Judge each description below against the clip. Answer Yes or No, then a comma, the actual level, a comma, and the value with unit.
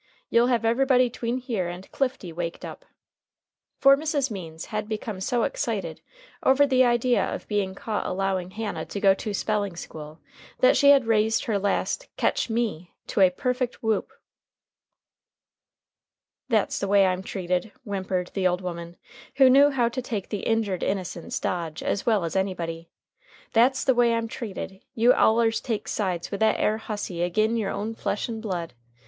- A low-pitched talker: No, high, 215 Hz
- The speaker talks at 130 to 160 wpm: No, average, 170 wpm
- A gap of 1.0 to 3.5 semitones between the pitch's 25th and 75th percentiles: No, average, 4.2 semitones